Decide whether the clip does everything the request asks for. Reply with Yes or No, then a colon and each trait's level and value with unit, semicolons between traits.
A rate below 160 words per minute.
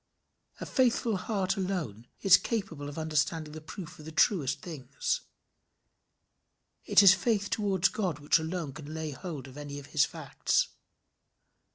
Yes: average, 150 wpm